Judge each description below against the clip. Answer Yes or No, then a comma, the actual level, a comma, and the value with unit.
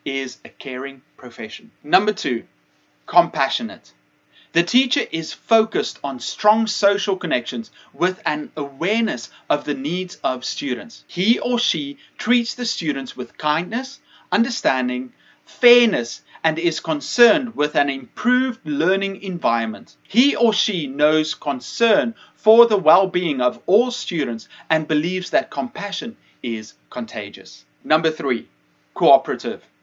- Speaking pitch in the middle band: Yes, medium, 175 Hz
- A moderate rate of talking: No, slow, 125 wpm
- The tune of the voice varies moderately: No, wide, 7.6 semitones